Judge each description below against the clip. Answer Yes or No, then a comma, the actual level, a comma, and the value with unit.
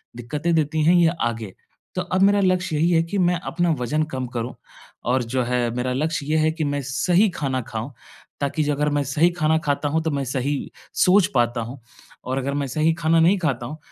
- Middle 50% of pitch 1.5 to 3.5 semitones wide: No, average, 4.2 semitones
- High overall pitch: No, medium, 150 Hz